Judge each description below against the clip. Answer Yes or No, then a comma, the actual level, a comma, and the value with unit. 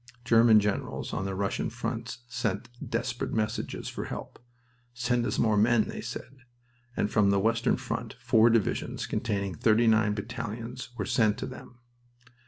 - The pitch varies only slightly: Yes, narrow, 2.3 semitones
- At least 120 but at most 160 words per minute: Yes, average, 155 wpm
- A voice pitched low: Yes, low, 115 Hz